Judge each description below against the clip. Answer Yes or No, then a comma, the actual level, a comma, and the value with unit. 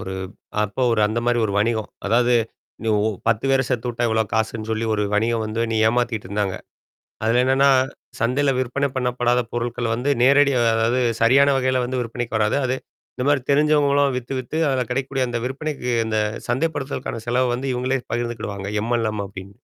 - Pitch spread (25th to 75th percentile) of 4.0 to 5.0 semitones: No, average, 2.8 semitones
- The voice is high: No, low, 120 Hz